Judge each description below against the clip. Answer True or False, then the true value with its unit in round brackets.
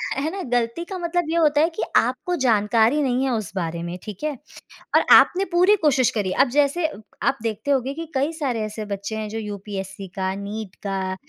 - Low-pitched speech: False (235 Hz)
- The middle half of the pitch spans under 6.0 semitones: False (6.7 semitones)